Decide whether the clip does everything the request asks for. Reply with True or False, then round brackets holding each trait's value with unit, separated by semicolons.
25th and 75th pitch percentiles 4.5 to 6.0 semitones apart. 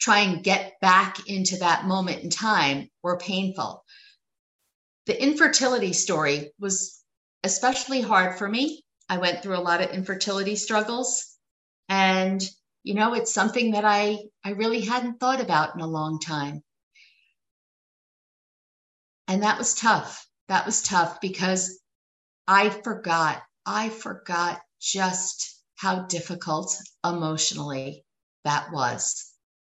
False (3.5 semitones)